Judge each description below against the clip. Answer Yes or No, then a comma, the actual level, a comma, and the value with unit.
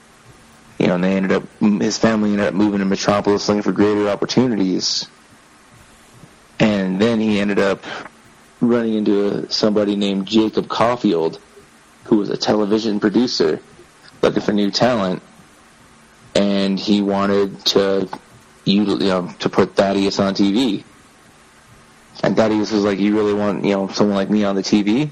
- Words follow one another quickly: No, average, 150 wpm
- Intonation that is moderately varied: No, narrow, 1.2 semitones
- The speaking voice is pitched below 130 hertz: Yes, low, 100 Hz